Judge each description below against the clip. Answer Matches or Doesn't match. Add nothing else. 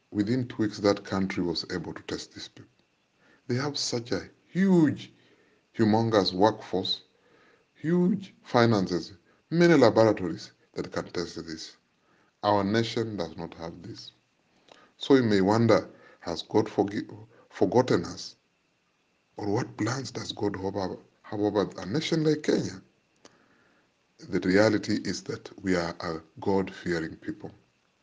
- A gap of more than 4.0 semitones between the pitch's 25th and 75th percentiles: Matches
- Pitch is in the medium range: Doesn't match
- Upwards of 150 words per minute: Doesn't match